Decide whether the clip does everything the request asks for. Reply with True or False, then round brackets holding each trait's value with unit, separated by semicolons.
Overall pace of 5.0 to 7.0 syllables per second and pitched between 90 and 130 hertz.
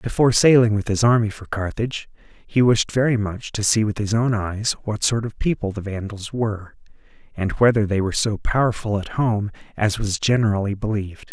True (5.5 syllables/s; 105 Hz)